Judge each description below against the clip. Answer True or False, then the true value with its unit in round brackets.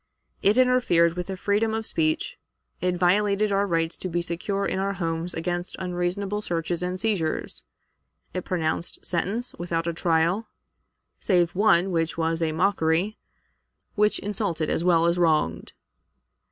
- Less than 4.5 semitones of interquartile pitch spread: True (3.2 semitones)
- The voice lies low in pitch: False (180 Hz)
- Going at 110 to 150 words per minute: True (145 wpm)